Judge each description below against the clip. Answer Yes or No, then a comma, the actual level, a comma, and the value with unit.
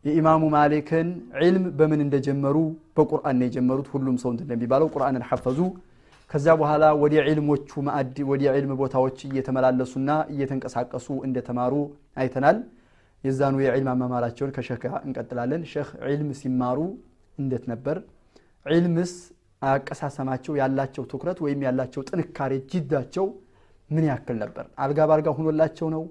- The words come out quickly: Yes, fast, 115 wpm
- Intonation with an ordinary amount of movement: Yes, average, 3.2 semitones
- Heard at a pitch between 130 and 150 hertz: Yes, medium, 140 Hz